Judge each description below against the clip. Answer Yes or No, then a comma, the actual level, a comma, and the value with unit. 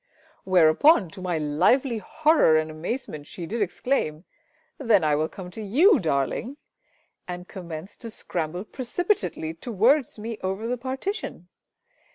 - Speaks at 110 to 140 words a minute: Yes, slow, 135 wpm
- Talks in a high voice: Yes, high, 195 Hz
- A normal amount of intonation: No, wide, 7.5 semitones